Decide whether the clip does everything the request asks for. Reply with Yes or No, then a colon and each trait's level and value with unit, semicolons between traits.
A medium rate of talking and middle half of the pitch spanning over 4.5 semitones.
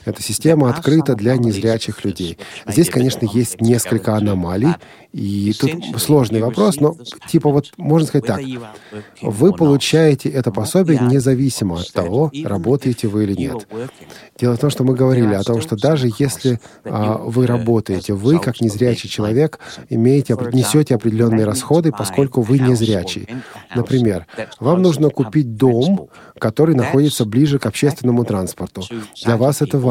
No: average, 145 wpm; average, 4.2 semitones